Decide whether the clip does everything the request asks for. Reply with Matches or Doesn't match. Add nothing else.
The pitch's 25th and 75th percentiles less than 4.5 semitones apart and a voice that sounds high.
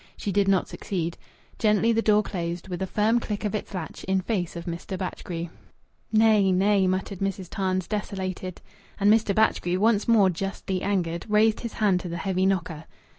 Matches